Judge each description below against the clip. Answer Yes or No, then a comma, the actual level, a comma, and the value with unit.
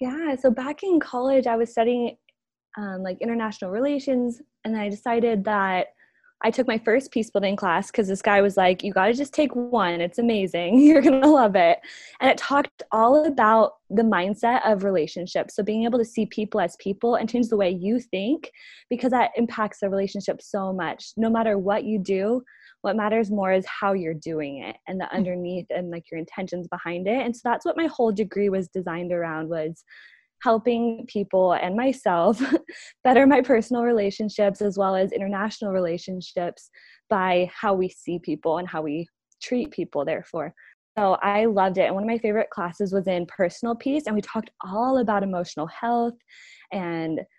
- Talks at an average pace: Yes, average, 190 wpm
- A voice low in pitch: No, high, 215 Hz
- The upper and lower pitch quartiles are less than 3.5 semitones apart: No, average, 4.4 semitones